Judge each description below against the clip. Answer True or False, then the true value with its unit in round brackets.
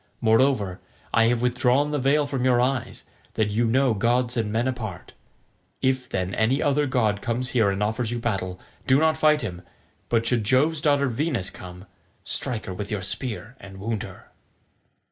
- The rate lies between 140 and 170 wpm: False (180 wpm)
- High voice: False (120 Hz)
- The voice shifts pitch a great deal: False (4.0 semitones)